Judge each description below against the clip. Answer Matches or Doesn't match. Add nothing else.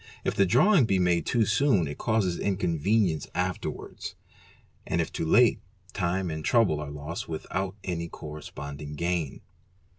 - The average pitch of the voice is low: Matches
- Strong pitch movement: Doesn't match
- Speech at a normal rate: Matches